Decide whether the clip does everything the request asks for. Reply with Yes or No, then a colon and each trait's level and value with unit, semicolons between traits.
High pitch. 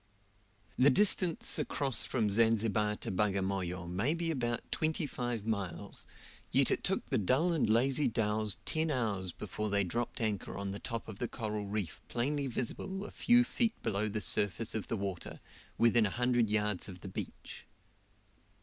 No: low, 110 Hz